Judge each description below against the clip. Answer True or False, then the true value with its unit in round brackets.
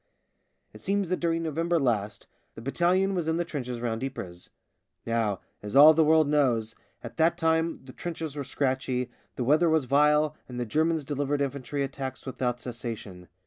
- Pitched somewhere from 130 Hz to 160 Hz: True (140 Hz)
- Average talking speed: True (175 wpm)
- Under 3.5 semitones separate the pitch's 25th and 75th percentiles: False (4.7 semitones)